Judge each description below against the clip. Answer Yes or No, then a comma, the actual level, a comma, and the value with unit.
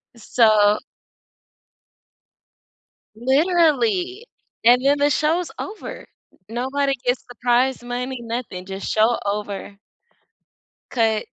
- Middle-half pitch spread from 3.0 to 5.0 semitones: Yes, average, 4.6 semitones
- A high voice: Yes, high, 245 Hz